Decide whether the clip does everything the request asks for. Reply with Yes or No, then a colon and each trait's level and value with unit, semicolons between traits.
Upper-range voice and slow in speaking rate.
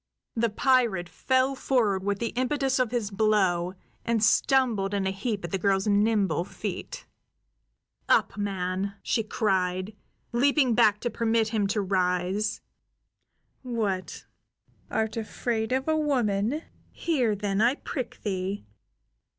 Yes: high, 215 Hz; slow, 130 wpm